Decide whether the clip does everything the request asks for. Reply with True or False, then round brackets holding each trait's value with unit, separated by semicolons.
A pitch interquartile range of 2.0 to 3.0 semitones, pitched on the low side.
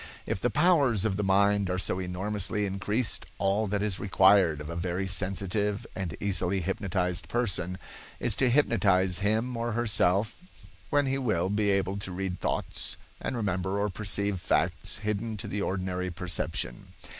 True (2.5 semitones; 100 Hz)